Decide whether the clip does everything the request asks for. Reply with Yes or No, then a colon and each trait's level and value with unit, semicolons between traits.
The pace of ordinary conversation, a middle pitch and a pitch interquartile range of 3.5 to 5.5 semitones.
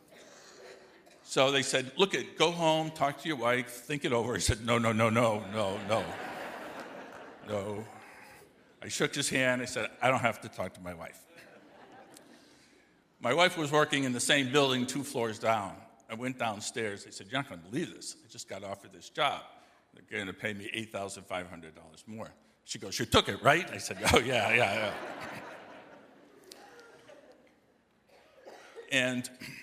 No: average, 170 wpm; low, 125 Hz; average, 4.4 semitones